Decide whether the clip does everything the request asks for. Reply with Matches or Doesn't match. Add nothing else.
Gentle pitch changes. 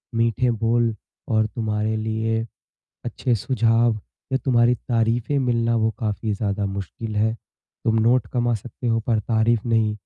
Matches